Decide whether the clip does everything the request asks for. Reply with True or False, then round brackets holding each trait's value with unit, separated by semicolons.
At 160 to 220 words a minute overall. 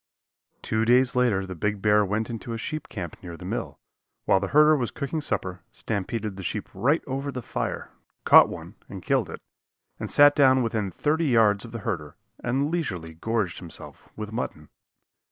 True (185 wpm)